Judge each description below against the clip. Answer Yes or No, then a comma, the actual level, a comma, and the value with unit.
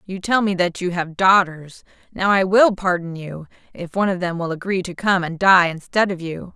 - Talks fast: Yes, fast, 230 wpm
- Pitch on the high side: No, medium, 180 Hz